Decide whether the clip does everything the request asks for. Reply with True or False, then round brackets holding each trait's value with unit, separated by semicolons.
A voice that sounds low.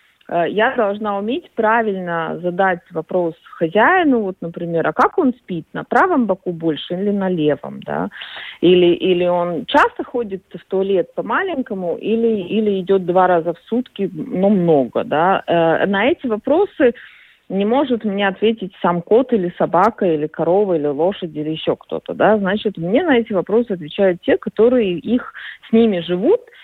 False (195 Hz)